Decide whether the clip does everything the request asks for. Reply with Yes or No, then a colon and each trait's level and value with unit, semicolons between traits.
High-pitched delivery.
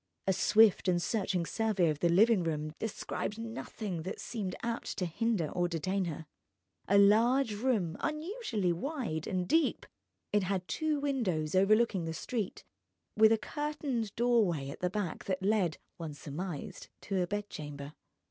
Yes: high, 200 Hz